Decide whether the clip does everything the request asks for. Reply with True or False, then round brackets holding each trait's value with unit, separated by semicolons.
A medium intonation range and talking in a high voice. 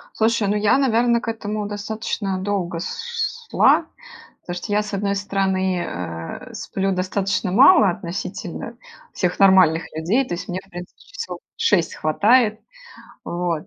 True (3.2 semitones; 195 Hz)